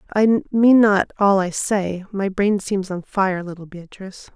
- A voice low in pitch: No, high, 195 Hz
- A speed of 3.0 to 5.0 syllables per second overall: Yes, 4.2 syllables/s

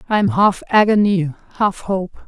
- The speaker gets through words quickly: No, average, 160 wpm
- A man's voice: No, female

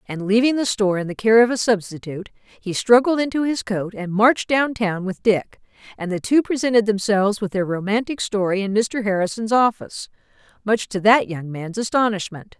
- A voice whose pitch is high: Yes, high, 210 Hz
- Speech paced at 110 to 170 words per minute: No, average, 190 wpm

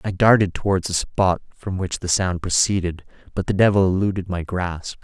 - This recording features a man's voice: Yes, male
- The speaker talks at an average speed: Yes, average, 190 wpm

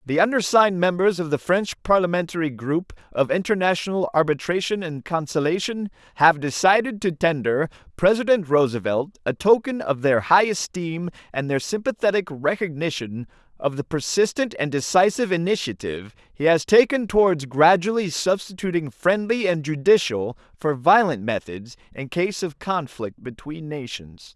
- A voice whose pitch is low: No, medium, 165 Hz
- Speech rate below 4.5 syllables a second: No, 5.0 syllables/s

